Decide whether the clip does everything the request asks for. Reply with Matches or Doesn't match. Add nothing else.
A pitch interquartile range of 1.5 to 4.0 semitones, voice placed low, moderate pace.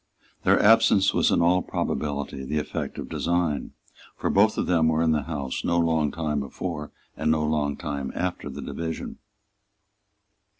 Matches